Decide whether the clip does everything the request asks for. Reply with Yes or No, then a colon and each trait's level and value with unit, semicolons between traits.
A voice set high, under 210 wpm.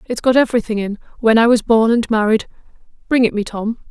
Yes: high, 225 Hz; average, 200 wpm